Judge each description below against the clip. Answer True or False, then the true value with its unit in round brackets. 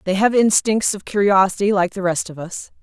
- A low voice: False (195 Hz)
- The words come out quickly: True (210 wpm)